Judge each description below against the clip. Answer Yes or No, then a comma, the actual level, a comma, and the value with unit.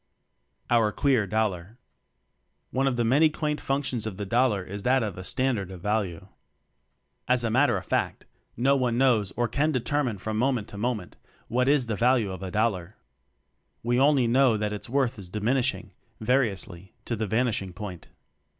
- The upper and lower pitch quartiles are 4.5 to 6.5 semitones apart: No, average, 4.0 semitones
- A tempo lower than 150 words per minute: No, average, 175 wpm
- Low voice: Yes, low, 115 Hz